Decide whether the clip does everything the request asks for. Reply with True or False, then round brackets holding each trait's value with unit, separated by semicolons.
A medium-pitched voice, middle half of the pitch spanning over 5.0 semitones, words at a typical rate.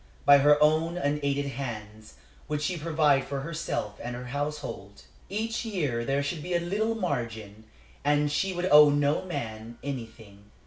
True (145 Hz; 5.4 semitones; 160 wpm)